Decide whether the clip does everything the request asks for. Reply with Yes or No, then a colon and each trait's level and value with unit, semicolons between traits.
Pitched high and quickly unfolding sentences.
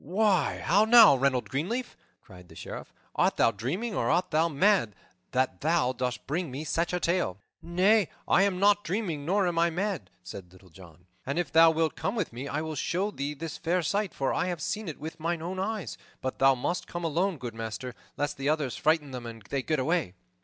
No: medium, 160 Hz; fast, 215 wpm